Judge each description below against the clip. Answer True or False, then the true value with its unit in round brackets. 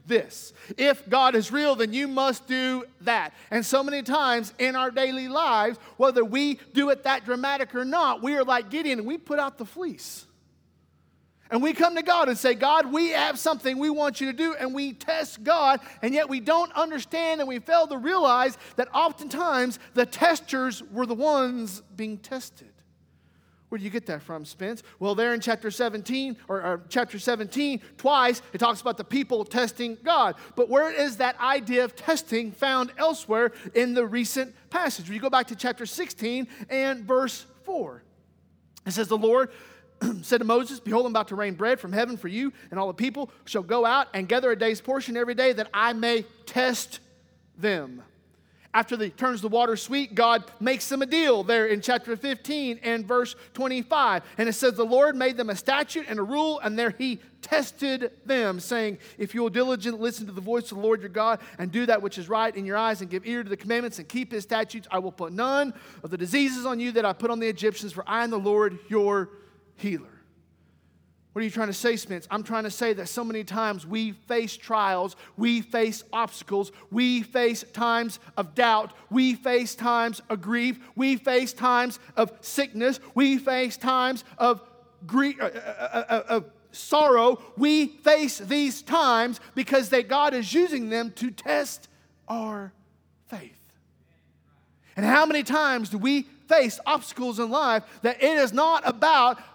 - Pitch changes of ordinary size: True (3.6 semitones)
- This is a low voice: False (240 Hz)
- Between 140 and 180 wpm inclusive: False (195 wpm)